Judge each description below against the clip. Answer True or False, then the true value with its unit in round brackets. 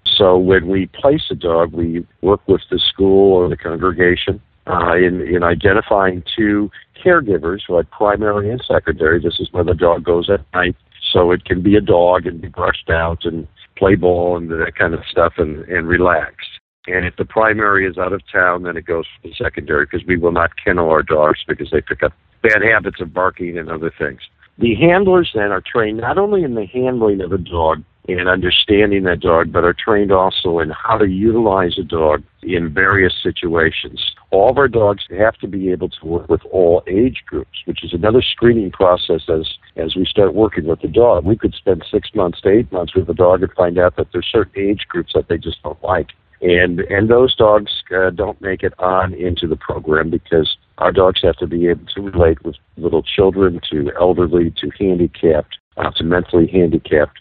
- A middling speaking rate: False (210 wpm)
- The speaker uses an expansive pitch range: False (2.7 semitones)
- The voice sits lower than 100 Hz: True (90 Hz)